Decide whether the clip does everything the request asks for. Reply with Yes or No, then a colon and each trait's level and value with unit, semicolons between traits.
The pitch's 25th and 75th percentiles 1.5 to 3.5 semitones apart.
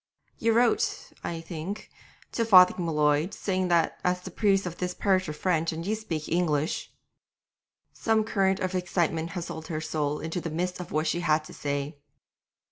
Yes: average, 3.0 semitones